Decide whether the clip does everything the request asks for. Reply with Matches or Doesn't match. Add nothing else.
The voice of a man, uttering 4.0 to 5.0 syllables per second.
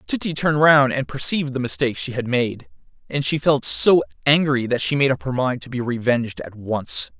Doesn't match